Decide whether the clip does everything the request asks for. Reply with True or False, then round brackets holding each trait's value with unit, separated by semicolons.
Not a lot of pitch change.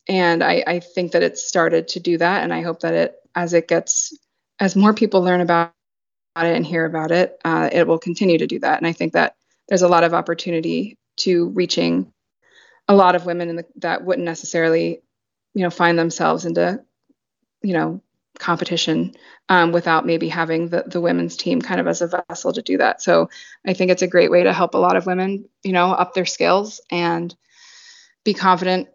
True (1.7 semitones)